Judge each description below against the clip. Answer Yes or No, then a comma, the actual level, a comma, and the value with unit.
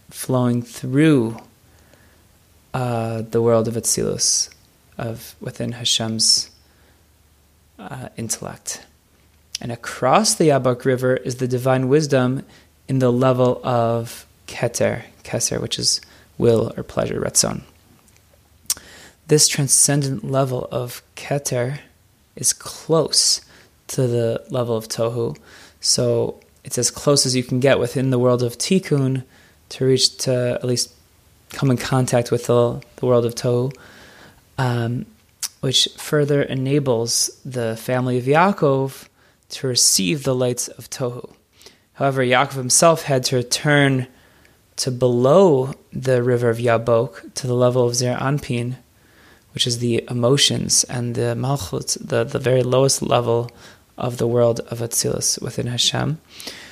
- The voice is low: Yes, low, 125 Hz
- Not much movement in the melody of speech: Yes, narrow, 2.3 semitones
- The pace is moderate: No, slow, 130 wpm